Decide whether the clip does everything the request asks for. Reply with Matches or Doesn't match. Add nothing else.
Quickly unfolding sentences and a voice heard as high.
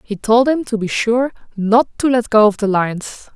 Matches